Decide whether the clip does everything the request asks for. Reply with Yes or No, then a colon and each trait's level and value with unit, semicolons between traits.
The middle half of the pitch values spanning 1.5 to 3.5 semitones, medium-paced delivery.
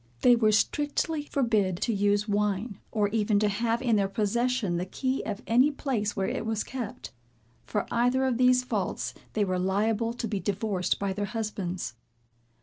Yes: average, 3.1 semitones; average, 175 wpm